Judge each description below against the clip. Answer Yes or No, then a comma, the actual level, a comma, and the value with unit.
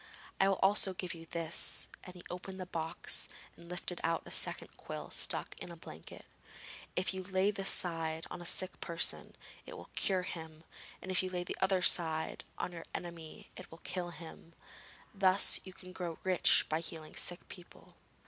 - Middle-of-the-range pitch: Yes, medium, 180 Hz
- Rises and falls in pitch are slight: Yes, narrow, 2.2 semitones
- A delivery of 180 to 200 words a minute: Yes, average, 185 wpm